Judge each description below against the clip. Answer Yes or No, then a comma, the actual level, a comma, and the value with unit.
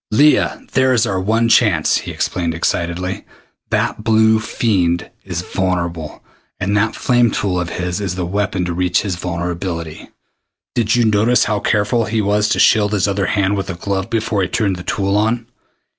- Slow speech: No, average, 180 wpm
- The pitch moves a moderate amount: Yes, average, 3.5 semitones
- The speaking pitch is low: Yes, low, 100 Hz